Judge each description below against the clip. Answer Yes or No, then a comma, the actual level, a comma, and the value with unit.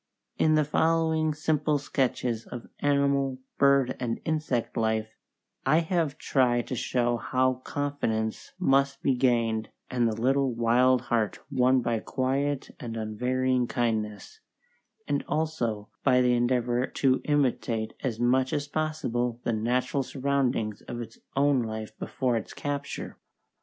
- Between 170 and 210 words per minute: No, slow, 135 wpm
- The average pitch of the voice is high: No, low, 130 Hz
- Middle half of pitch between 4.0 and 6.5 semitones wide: No, average, 3.0 semitones